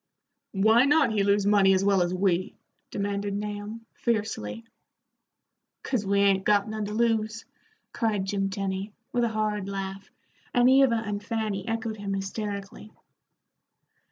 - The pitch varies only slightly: Yes, narrow, 2.0 semitones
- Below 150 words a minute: Yes, average, 140 wpm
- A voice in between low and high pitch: No, high, 205 Hz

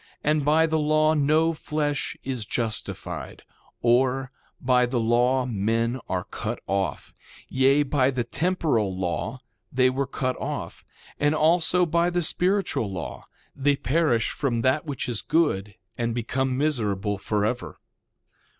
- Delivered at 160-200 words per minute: No, slow, 135 wpm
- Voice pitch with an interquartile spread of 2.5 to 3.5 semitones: No, average, 4.7 semitones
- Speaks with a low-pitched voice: Yes, low, 130 Hz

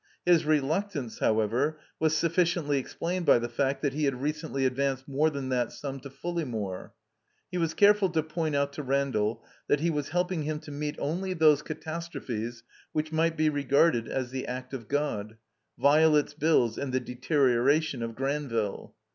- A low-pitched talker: No, medium, 145 Hz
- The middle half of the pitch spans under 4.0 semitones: Yes, average, 3.6 semitones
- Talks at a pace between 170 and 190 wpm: Yes, average, 175 wpm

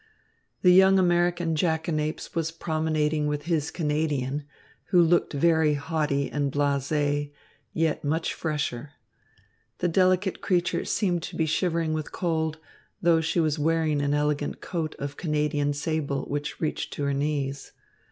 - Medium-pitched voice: Yes, medium, 155 Hz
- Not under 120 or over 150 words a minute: Yes, average, 140 wpm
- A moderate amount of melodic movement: No, narrow, 2.2 semitones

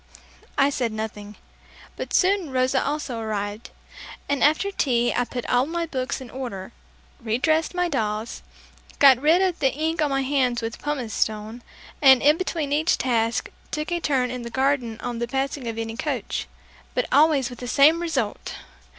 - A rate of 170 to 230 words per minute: Yes, average, 175 wpm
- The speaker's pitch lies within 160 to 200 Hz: No, very high, 260 Hz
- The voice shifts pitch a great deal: No, average, 4.3 semitones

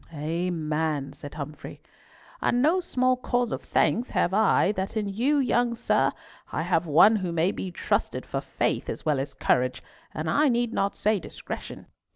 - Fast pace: No, average, 175 wpm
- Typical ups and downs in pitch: No, wide, 7.3 semitones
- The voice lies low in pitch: No, high, 190 Hz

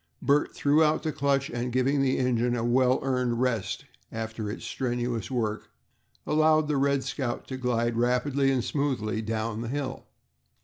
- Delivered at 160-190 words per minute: Yes, average, 165 wpm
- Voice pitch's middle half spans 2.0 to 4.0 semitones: Yes, average, 2.9 semitones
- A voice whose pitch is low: Yes, low, 125 Hz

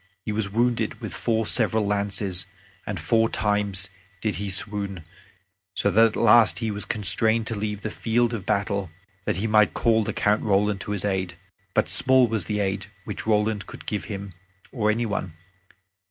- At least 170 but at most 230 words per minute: Yes, average, 185 wpm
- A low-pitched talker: Yes, low, 105 Hz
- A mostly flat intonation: Yes, narrow, 1.9 semitones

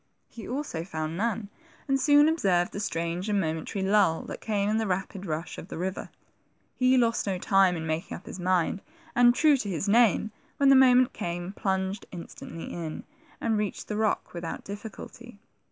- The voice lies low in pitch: No, high, 200 Hz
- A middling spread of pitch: Yes, average, 4.7 semitones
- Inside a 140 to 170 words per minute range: No, average, 185 wpm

